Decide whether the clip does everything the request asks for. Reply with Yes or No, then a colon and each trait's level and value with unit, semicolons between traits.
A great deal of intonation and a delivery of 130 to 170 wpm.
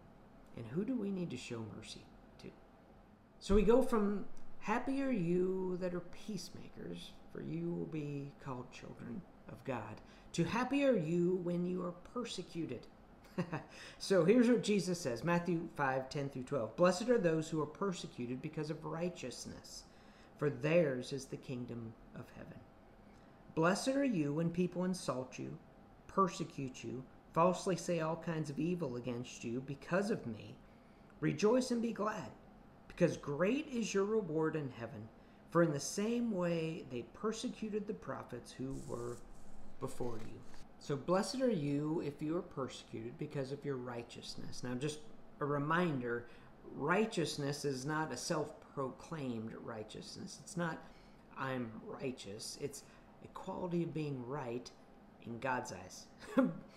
Yes: wide, 5.8 semitones; average, 150 wpm